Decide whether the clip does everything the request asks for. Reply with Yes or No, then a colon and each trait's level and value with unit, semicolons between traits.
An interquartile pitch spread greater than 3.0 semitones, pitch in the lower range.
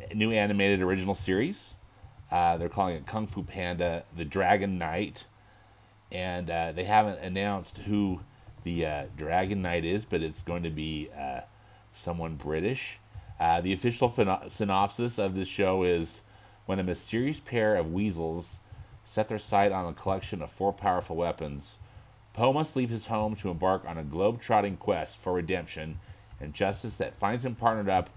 Yes: average, 3.4 semitones; low, 100 Hz